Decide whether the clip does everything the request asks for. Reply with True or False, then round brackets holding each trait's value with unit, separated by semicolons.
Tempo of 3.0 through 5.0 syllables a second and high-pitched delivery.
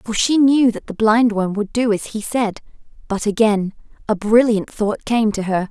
True (4.6 syllables/s; 220 Hz)